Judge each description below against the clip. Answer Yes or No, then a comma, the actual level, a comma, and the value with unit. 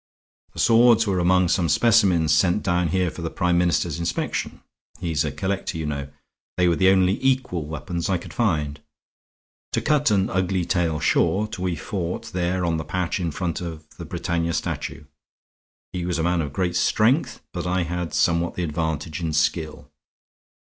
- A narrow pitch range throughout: Yes, narrow, 2.3 semitones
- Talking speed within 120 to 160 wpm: No, average, 180 wpm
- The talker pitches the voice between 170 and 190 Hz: No, very low, 90 Hz